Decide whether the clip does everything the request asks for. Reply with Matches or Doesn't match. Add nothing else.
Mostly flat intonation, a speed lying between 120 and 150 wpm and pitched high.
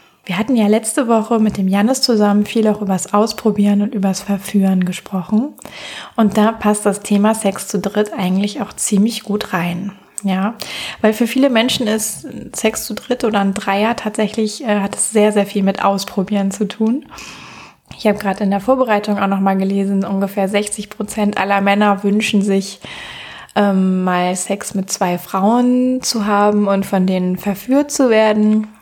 Doesn't match